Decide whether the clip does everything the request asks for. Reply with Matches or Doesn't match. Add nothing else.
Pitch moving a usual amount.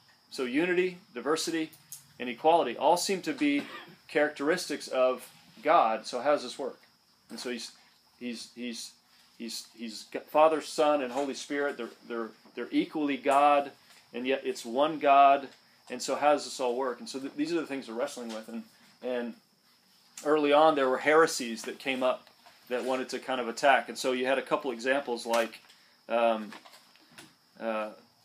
Matches